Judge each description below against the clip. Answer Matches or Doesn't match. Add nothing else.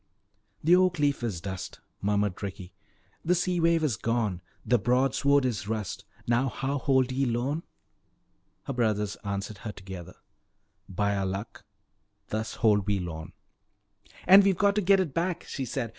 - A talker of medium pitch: Doesn't match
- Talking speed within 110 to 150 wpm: Doesn't match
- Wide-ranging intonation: Matches